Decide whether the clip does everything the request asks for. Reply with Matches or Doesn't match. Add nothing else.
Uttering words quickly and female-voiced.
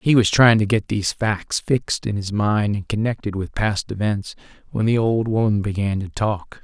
Doesn't match